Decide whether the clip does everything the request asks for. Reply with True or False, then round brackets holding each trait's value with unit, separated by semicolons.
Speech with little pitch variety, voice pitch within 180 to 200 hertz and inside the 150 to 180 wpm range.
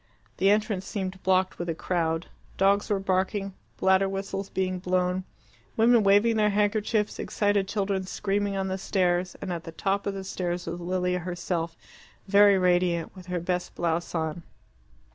True (2.0 semitones; 190 Hz; 160 wpm)